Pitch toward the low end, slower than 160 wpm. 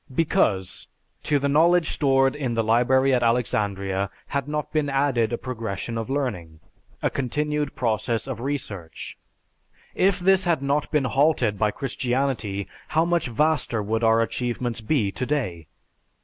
Yes: low, 130 Hz; average, 145 wpm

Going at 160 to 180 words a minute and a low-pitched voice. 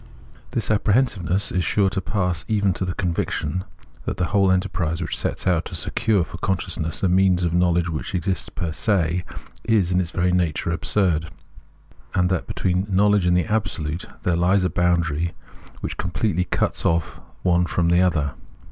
Yes: average, 175 wpm; very low, 90 Hz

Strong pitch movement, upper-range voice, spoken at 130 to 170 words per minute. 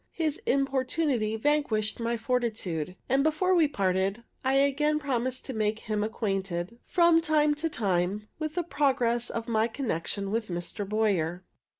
Yes: wide, 5.7 semitones; high, 235 Hz; average, 150 wpm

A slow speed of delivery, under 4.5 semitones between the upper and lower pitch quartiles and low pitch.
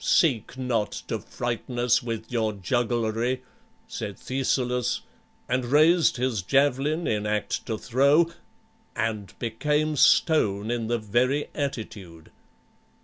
Yes: slow, 115 wpm; average, 3.7 semitones; low, 120 Hz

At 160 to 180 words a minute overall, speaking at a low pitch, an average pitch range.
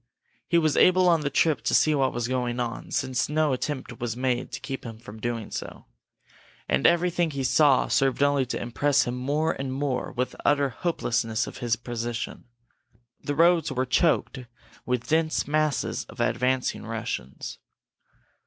Yes: average, 170 wpm; low, 130 Hz; average, 3.9 semitones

